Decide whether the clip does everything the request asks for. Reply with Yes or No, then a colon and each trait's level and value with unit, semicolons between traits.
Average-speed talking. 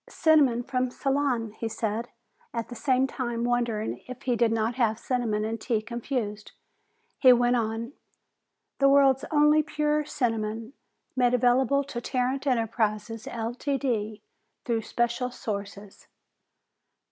No: slow, 125 wpm